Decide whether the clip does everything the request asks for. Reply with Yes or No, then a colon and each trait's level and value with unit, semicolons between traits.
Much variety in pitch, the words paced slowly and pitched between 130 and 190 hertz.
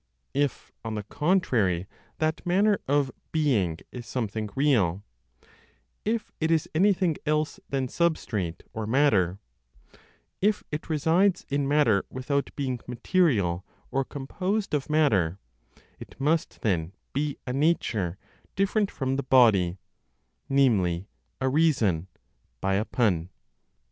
Yes: wide, 7.1 semitones; slow, 120 wpm; low, 135 Hz